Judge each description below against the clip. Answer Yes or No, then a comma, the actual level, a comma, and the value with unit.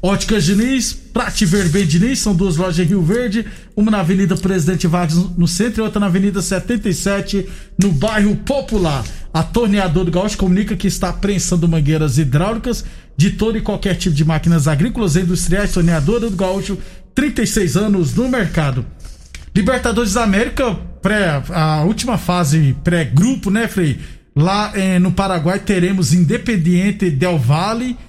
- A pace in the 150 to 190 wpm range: Yes, average, 160 wpm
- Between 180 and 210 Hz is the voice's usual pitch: Yes, high, 190 Hz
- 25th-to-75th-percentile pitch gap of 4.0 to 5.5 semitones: No, average, 3.3 semitones